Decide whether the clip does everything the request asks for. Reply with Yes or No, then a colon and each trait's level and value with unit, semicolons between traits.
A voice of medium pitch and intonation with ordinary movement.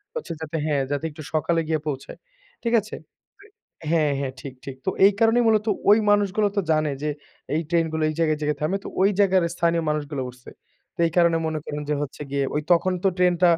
Yes: medium, 160 Hz; average, 3.8 semitones